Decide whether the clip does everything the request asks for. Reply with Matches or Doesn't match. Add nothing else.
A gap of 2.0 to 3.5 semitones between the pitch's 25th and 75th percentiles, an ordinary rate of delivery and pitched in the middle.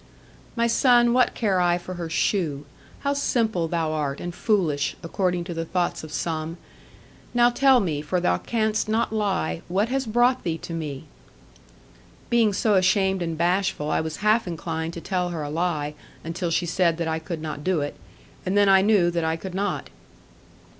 Doesn't match